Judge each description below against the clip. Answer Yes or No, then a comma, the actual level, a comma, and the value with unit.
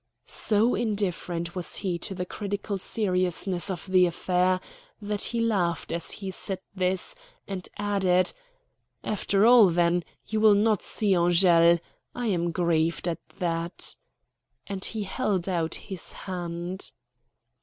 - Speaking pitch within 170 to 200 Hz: Yes, medium, 185 Hz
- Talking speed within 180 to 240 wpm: No, slow, 135 wpm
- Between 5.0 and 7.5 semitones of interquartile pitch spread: No, average, 2.9 semitones